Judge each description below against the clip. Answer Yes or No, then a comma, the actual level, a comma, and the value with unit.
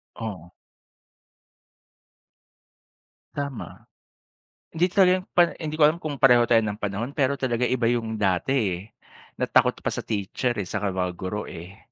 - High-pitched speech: No, low, 115 Hz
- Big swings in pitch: Yes, wide, 5.8 semitones